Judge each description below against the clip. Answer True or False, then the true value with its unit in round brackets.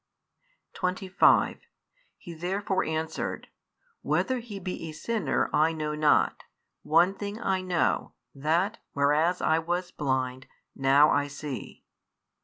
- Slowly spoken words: True (115 wpm)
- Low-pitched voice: False (165 Hz)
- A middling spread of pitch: True (3.8 semitones)